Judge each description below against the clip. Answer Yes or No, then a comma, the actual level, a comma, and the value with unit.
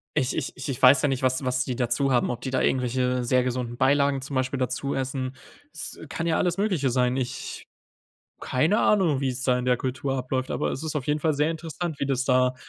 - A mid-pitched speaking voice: No, low, 130 Hz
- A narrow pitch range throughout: Yes, narrow, 1.9 semitones